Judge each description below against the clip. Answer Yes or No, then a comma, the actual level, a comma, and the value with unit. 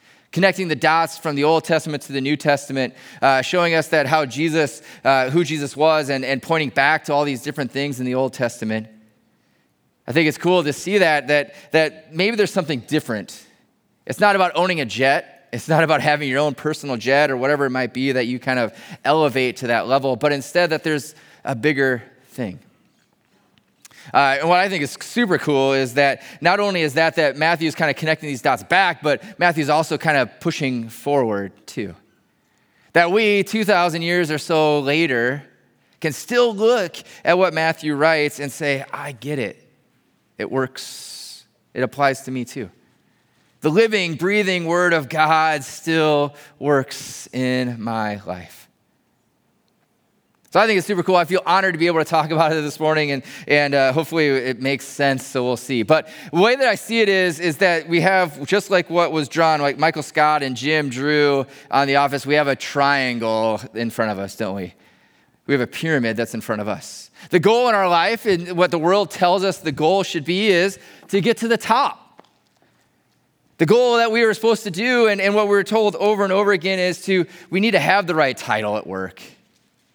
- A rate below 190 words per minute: No, fast, 205 wpm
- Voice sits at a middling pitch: Yes, medium, 155 Hz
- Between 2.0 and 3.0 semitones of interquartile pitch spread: No, average, 4.5 semitones